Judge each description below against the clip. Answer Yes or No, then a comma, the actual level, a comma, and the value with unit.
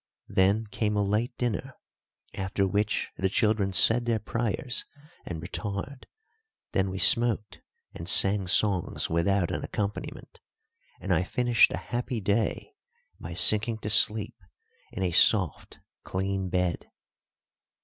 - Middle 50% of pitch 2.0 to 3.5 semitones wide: Yes, average, 2.8 semitones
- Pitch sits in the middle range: No, low, 105 Hz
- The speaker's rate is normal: No, slow, 130 wpm